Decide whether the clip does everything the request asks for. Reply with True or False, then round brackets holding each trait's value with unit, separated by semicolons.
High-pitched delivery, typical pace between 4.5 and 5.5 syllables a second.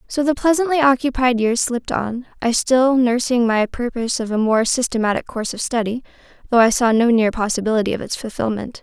False (240 Hz; 5.8 syllables/s)